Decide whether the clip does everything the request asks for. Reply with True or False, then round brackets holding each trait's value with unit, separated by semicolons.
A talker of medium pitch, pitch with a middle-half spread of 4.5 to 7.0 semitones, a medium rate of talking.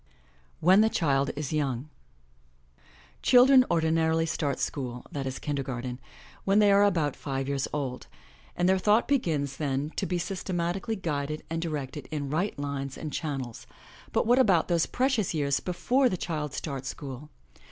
True (155 Hz; 4.9 semitones; 165 wpm)